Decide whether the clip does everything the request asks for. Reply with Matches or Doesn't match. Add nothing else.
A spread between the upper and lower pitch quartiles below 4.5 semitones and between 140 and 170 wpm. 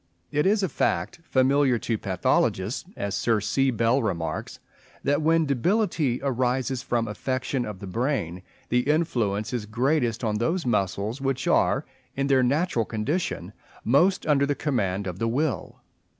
Doesn't match